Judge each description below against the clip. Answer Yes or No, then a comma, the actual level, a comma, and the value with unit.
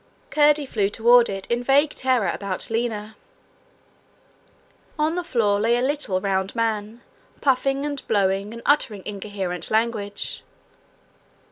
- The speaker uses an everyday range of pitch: Yes, average, 4.6 semitones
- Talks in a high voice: Yes, high, 225 Hz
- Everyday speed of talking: No, slow, 125 wpm